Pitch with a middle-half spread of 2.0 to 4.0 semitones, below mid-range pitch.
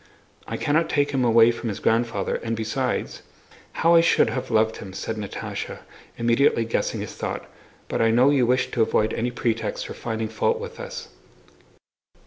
Yes: average, 3.2 semitones; low, 115 Hz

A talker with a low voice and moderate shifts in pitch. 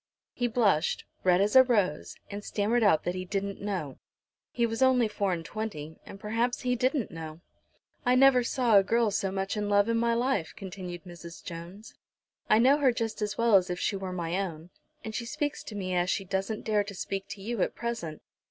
No: high, 205 Hz; average, 4.2 semitones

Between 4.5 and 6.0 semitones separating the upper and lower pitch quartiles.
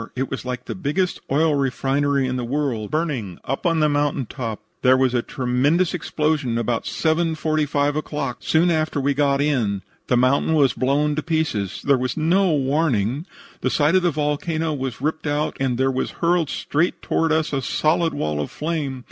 No: average, 3.4 semitones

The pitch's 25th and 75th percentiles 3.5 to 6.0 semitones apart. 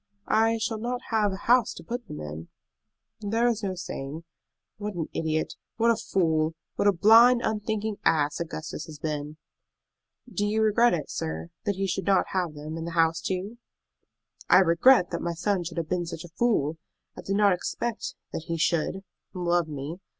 Yes: average, 5.1 semitones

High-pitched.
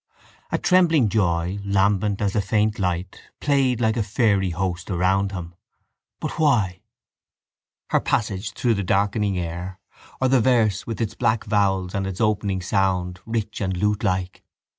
No: low, 100 Hz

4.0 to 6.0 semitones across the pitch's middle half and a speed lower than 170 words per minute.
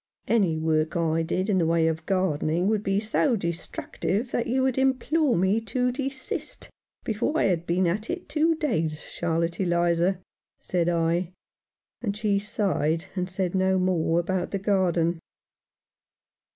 Yes: average, 4.5 semitones; average, 155 wpm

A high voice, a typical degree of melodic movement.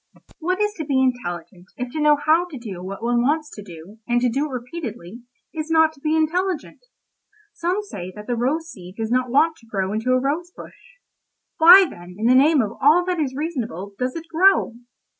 No: very high, 265 Hz; wide, 6.3 semitones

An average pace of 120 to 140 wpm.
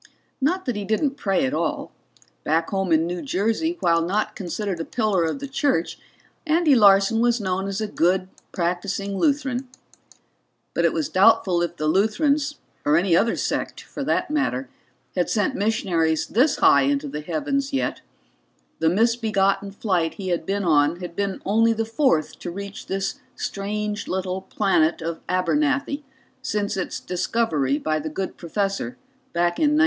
No: average, 165 wpm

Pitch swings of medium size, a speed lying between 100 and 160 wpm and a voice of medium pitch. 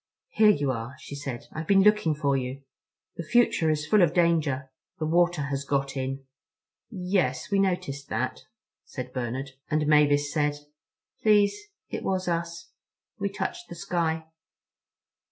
Yes: average, 4.7 semitones; average, 150 wpm; medium, 155 Hz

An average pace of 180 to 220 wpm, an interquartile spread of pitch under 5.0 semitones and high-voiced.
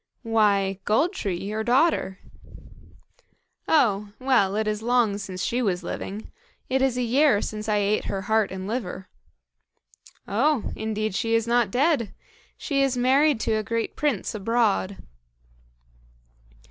No: average, 140 wpm; average, 3.7 semitones; high, 220 Hz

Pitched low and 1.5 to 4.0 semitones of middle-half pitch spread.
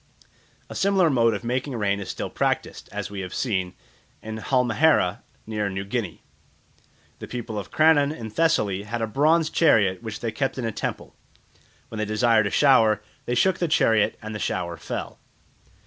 No: low, 115 Hz; average, 4.6 semitones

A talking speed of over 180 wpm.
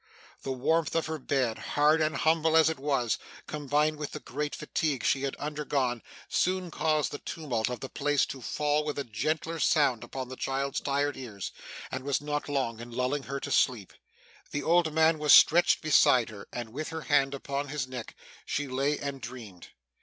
Yes: average, 190 wpm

